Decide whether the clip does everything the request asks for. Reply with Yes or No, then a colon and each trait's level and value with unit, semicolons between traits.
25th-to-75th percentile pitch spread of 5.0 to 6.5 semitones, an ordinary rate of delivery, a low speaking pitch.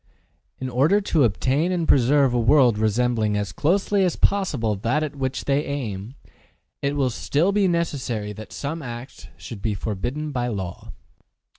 Yes: average, 5.3 semitones; average, 160 wpm; low, 130 Hz